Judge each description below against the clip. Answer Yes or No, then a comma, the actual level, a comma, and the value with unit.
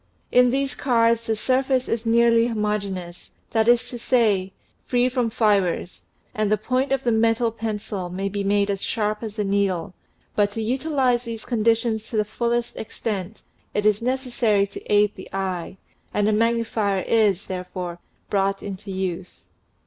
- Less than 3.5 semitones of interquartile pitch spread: Yes, average, 3.0 semitones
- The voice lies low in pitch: No, high, 215 Hz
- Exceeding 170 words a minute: No, average, 165 wpm